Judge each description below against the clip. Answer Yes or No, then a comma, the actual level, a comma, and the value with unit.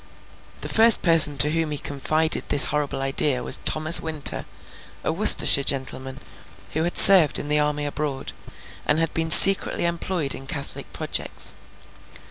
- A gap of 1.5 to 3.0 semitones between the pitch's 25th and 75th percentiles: Yes, narrow, 2.6 semitones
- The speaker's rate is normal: Yes, average, 150 wpm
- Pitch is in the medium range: Yes, medium, 150 Hz